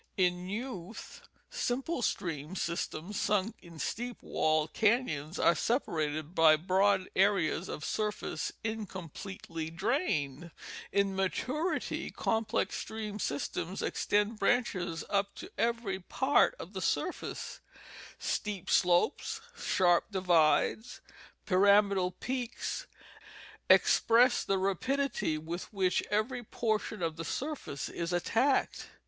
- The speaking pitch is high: Yes, high, 195 Hz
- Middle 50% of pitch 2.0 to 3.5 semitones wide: No, average, 4.9 semitones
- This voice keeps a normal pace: No, slow, 105 wpm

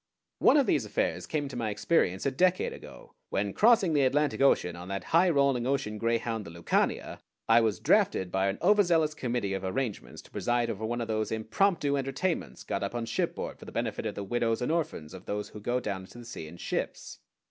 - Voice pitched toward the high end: No, low, 120 Hz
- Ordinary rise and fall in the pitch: No, wide, 5.9 semitones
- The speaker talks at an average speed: No, fast, 215 wpm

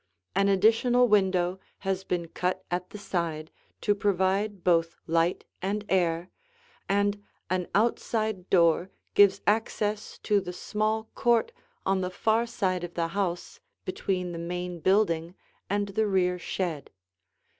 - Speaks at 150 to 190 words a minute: No, slow, 135 wpm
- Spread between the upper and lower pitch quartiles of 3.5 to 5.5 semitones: No, average, 2.7 semitones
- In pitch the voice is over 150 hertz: Yes, high, 190 Hz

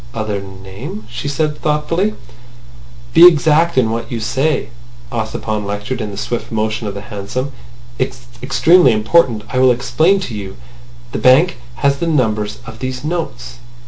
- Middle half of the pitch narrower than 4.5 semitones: No, wide, 5.6 semitones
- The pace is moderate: Yes, average, 155 wpm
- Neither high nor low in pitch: No, low, 120 Hz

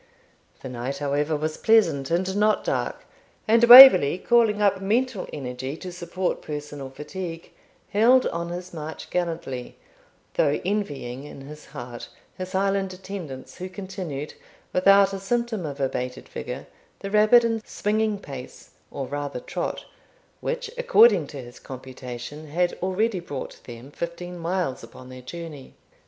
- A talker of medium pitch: Yes, medium, 175 Hz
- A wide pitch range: Yes, wide, 6.2 semitones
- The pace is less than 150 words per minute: Yes, average, 140 wpm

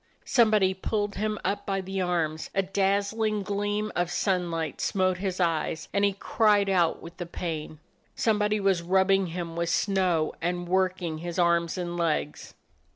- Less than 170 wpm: Yes, average, 160 wpm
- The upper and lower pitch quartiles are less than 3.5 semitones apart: Yes, average, 2.8 semitones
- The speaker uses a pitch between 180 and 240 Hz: Yes, medium, 185 Hz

